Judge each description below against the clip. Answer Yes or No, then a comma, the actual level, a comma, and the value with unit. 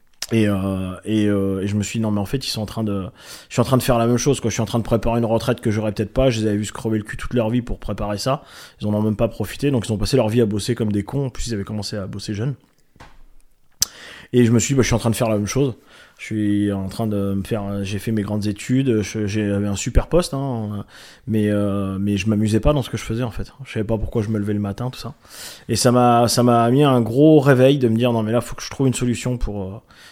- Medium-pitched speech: No, low, 110 Hz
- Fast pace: Yes, fast, 315 wpm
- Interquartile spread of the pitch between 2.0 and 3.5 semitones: Yes, average, 3.1 semitones